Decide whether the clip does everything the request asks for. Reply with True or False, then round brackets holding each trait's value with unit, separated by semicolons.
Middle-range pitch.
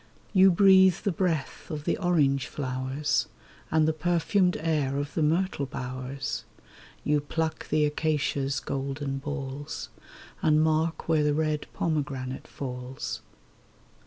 True (150 Hz)